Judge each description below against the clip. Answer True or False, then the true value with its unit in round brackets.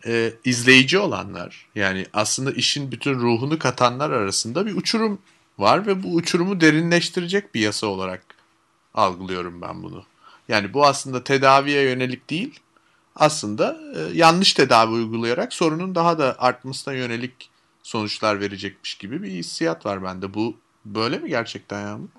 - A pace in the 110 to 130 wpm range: False (140 wpm)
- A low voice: True (125 Hz)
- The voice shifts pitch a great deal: True (7.3 semitones)